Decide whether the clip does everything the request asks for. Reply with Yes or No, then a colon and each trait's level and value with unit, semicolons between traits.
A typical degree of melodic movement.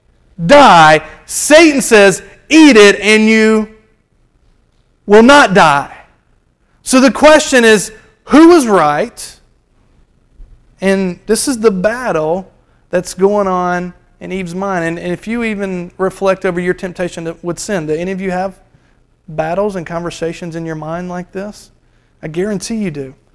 Yes: average, 4.0 semitones